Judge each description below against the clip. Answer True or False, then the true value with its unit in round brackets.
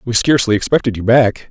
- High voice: False (115 Hz)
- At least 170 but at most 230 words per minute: True (200 wpm)